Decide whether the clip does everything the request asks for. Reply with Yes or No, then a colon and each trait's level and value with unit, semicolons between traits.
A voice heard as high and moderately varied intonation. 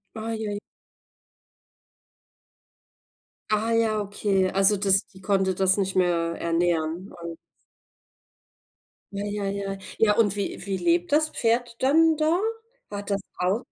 Yes: high, 200 Hz; average, 3.2 semitones